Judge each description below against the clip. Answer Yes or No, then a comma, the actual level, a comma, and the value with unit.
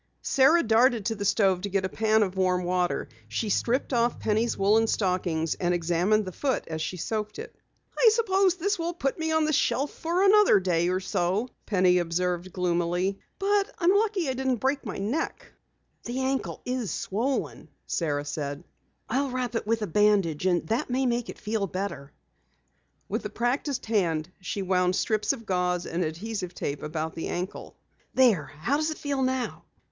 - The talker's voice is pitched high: Yes, high, 210 Hz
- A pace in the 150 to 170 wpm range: No, average, 185 wpm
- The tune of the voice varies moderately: No, wide, 6.5 semitones